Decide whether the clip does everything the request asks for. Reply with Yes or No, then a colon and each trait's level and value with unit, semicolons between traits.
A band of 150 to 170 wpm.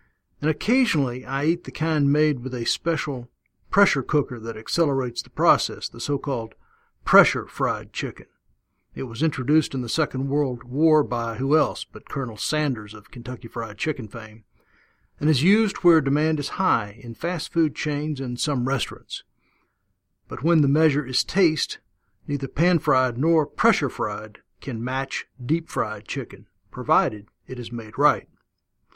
Yes: average, 155 wpm